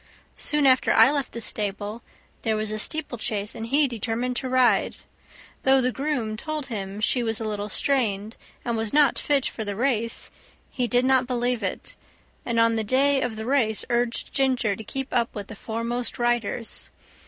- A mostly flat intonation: No, average, 3.0 semitones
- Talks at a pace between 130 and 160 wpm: No, average, 185 wpm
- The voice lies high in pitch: Yes, high, 235 Hz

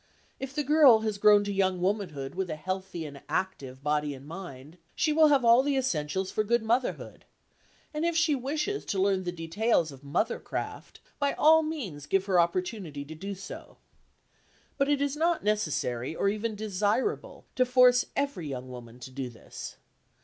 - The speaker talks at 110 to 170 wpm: No, average, 180 wpm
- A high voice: Yes, high, 200 Hz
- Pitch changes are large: Yes, wide, 8.4 semitones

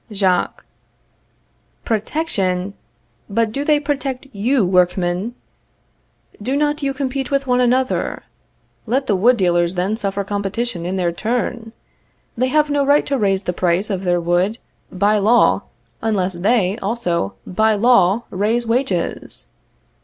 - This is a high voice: Yes, high, 215 Hz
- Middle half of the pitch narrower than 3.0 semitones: No, average, 5.3 semitones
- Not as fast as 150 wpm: Yes, slow, 135 wpm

